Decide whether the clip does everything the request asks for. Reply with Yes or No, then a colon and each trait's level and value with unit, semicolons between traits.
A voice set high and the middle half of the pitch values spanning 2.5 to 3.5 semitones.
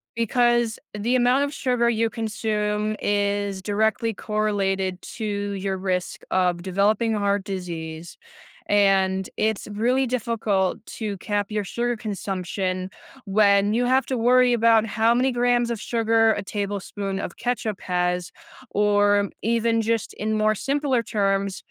Yes: high, 210 Hz; average, 2.8 semitones